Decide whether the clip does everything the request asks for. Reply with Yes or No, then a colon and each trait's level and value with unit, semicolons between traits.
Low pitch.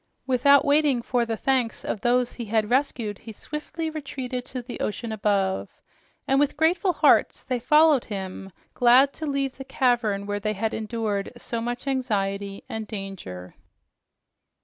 No: high, 240 Hz